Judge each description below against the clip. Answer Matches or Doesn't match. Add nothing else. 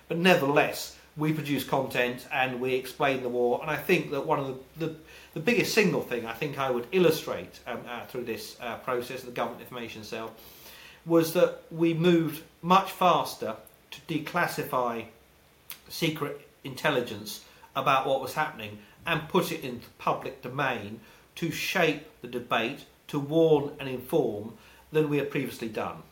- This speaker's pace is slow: Doesn't match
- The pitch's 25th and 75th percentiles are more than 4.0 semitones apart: Matches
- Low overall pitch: Doesn't match